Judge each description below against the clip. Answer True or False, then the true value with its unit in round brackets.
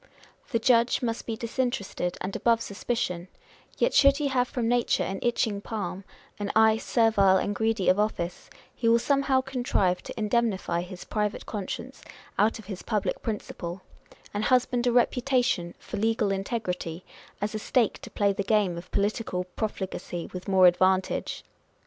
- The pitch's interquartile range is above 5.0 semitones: False (3.8 semitones)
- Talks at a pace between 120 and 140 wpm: False (160 wpm)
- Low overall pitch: False (215 Hz)